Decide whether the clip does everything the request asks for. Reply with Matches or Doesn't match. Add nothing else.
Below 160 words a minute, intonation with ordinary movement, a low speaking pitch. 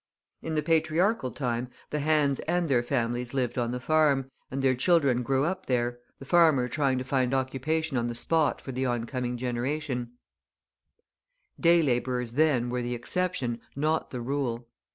Doesn't match